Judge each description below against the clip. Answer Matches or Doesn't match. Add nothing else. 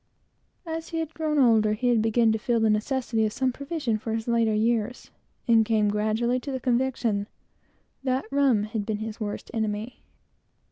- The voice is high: Matches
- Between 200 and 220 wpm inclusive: Doesn't match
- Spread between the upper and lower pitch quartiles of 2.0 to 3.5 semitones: Matches